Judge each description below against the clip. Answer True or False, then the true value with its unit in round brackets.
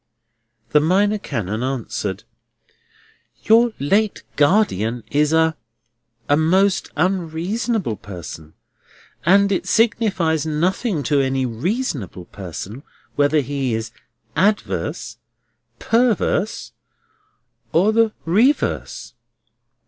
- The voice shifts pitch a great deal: True (8.9 semitones)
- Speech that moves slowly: True (85 wpm)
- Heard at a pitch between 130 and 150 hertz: False (160 Hz)